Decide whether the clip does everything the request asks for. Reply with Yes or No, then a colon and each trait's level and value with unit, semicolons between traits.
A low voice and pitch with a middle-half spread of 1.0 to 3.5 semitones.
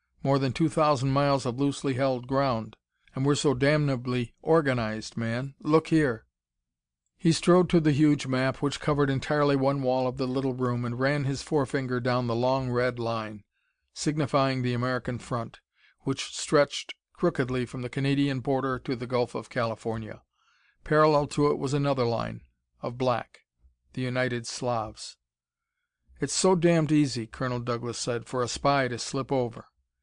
Yes: low, 130 Hz; average, 3.0 semitones